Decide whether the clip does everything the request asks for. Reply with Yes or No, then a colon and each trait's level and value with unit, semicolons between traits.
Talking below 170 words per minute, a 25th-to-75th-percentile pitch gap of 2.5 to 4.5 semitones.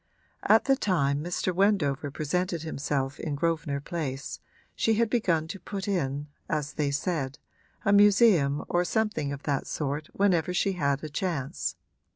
No: average, 155 wpm; average, 5.2 semitones